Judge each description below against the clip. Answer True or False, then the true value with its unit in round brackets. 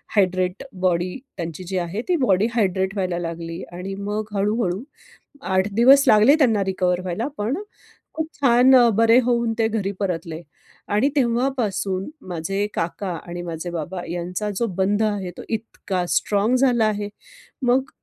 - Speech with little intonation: False (4.1 semitones)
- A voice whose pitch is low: False (200 Hz)